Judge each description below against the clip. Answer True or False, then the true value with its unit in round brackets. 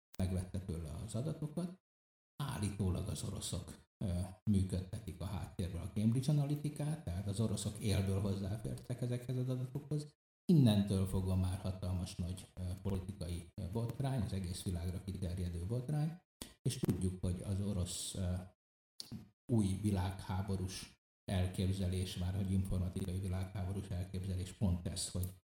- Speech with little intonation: False (3.3 semitones)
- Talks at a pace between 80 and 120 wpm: True (115 wpm)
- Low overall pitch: True (95 Hz)